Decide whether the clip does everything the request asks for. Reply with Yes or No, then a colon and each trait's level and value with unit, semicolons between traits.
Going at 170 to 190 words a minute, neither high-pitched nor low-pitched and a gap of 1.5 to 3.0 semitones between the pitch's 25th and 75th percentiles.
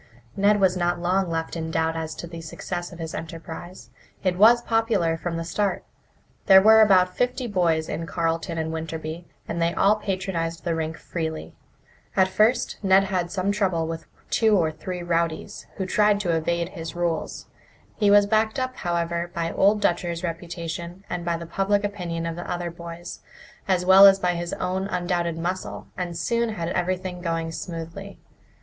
Yes: average, 180 wpm; medium, 175 Hz; average, 2.7 semitones